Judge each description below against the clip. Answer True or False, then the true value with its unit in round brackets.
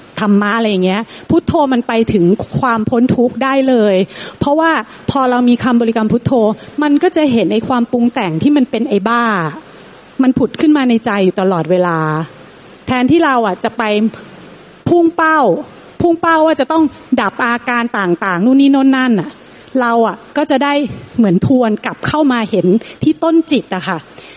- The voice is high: True (240 Hz)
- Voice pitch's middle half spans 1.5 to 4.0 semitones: False (4.5 semitones)